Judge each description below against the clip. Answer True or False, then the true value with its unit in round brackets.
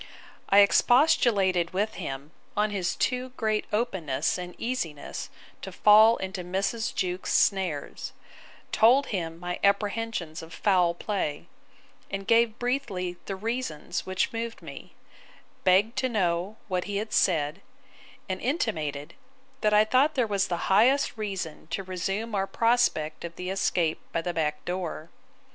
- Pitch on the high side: True (195 Hz)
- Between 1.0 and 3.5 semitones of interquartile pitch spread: False (4.2 semitones)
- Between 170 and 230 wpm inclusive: False (140 wpm)